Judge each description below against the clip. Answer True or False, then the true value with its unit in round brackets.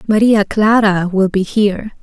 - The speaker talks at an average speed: True (150 wpm)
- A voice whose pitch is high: True (205 Hz)